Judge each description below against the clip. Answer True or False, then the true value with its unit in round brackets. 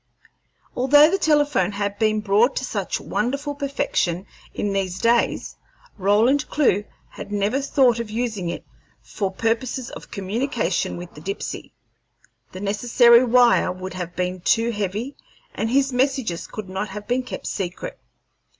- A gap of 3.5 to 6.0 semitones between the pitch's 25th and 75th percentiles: True (4.7 semitones)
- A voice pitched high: True (220 Hz)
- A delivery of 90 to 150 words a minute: True (145 wpm)